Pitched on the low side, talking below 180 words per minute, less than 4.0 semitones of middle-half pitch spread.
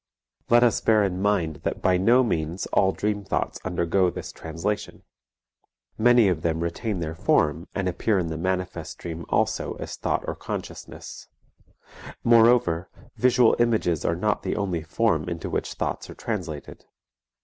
No: very low, 95 Hz; average, 155 wpm; average, 4.6 semitones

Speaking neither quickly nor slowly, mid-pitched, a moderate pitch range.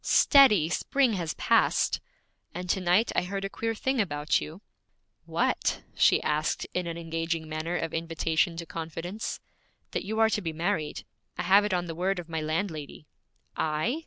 Yes: average, 175 wpm; medium, 170 Hz; average, 3.7 semitones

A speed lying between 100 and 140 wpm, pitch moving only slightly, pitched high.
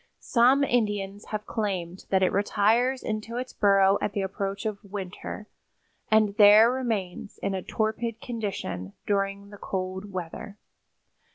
Yes: slow, 135 wpm; narrow, 2.1 semitones; high, 205 Hz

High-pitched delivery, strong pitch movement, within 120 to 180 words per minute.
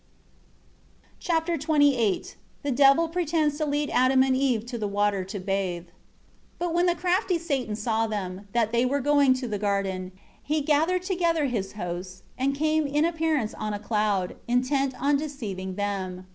Yes: very high, 255 Hz; wide, 6.8 semitones; average, 170 wpm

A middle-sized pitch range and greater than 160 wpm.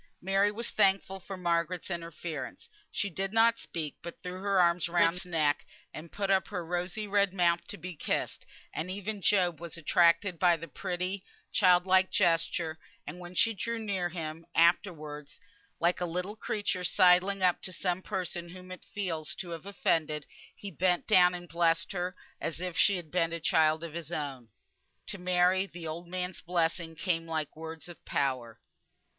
No: narrow, 2.2 semitones; average, 180 wpm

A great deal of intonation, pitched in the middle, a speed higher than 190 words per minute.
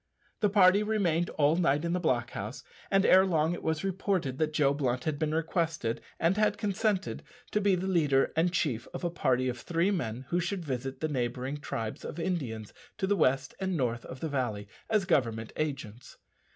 Yes: wide, 6.0 semitones; medium, 155 Hz; average, 200 wpm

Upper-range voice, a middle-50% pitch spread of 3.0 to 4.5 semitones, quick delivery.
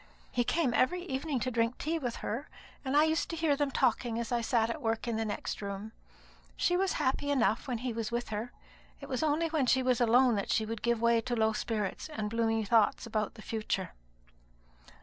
Yes: high, 240 Hz; average, 3.7 semitones; fast, 220 wpm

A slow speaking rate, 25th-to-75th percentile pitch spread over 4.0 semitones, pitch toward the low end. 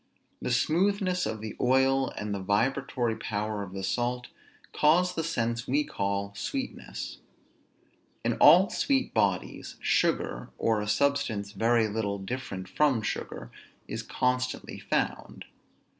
Yes: slow, 130 wpm; wide, 5.4 semitones; low, 120 Hz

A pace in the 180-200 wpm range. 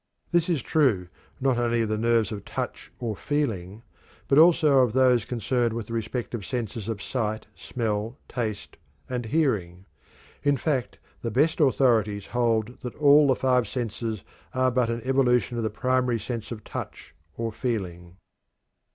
No: average, 160 wpm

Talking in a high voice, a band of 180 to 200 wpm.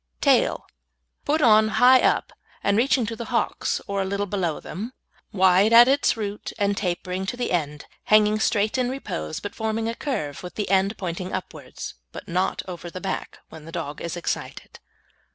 Yes: high, 200 Hz; average, 185 wpm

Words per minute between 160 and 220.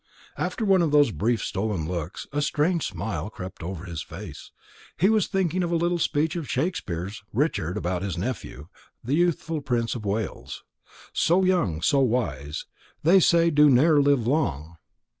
Yes: average, 165 wpm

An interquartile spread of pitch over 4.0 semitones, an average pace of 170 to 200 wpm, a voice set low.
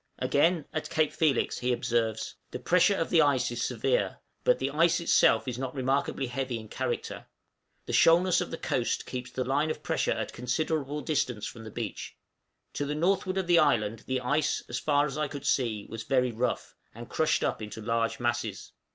Yes: average, 4.5 semitones; average, 195 wpm; low, 130 Hz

